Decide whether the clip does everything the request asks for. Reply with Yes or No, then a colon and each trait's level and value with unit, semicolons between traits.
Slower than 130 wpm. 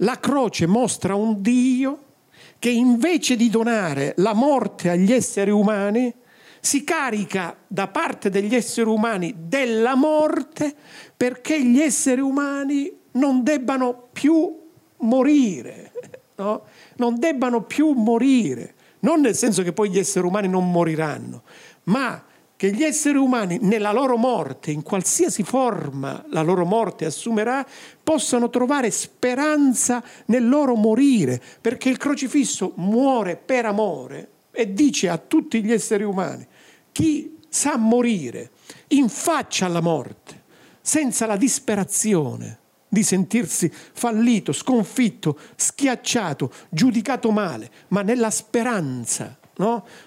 Yes: average, 120 wpm